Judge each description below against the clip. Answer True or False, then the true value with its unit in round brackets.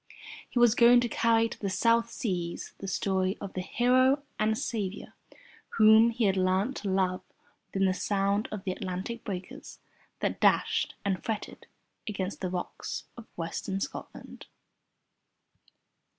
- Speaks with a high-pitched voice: True (200 Hz)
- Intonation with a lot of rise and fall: False (3.5 semitones)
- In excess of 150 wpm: False (145 wpm)